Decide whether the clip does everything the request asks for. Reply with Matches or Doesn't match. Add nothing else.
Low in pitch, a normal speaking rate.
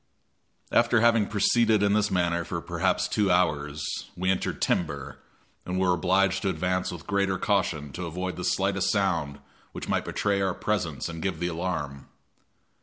Matches